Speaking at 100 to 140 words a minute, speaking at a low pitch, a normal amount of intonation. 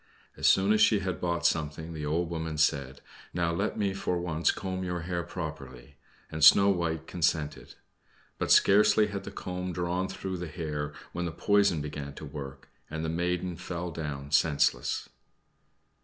No: average, 170 wpm; very low, 85 Hz; average, 3.1 semitones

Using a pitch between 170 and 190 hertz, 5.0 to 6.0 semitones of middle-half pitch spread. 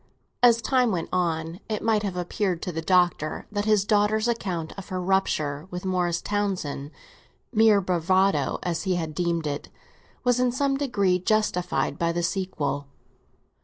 No: medium, 185 Hz; average, 3.8 semitones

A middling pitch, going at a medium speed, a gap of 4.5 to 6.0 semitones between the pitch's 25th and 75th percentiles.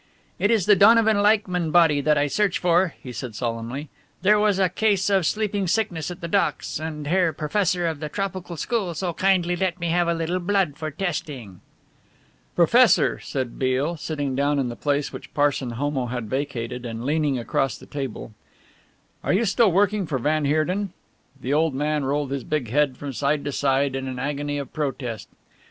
Yes: medium, 150 Hz; average, 190 wpm; average, 4.9 semitones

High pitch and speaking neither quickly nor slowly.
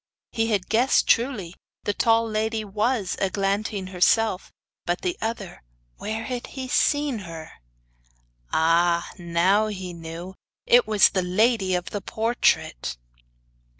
No: high, 205 Hz; slow, 125 wpm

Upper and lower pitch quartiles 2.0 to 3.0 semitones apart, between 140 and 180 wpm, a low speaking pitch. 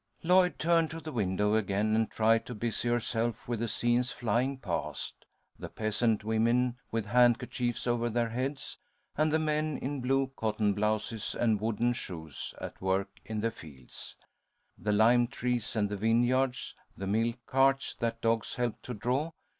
Yes: narrow, 2.6 semitones; average, 160 wpm; low, 115 Hz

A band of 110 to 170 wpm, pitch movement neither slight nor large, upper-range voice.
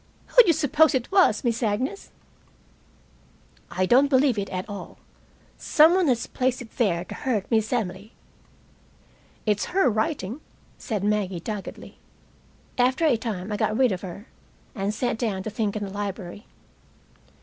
Yes: average, 155 wpm; average, 4.4 semitones; high, 220 Hz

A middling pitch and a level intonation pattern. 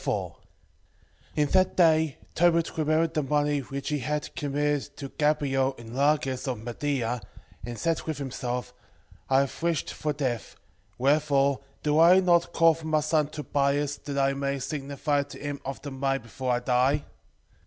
Yes: medium, 145 Hz; narrow, 2.2 semitones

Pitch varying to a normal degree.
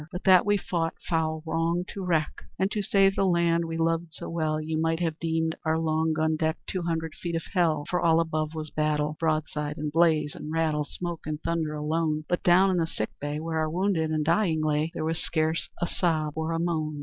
No: narrow, 1.6 semitones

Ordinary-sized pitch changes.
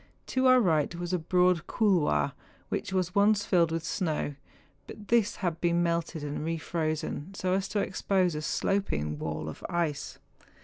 Yes: average, 3.5 semitones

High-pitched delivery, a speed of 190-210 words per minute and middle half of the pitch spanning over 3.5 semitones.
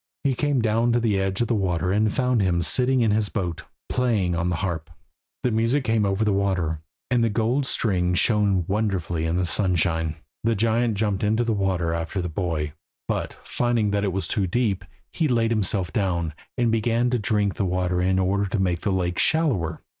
No: low, 100 Hz; fast, 205 wpm; average, 4.3 semitones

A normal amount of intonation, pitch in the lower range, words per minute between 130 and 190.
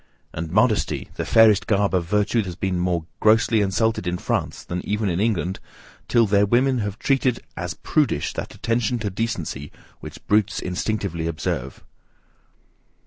Yes: average, 4.0 semitones; low, 100 Hz; average, 150 wpm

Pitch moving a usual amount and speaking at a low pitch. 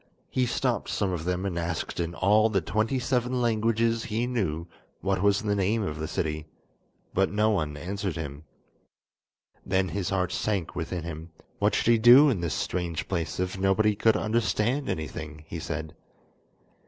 Yes: average, 4.7 semitones; very low, 95 Hz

